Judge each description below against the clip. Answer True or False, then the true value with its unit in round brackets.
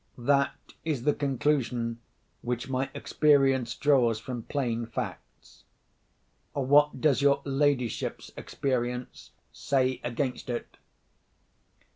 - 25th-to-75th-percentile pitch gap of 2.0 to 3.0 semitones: True (2.6 semitones)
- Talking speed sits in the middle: False (95 wpm)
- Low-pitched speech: True (130 Hz)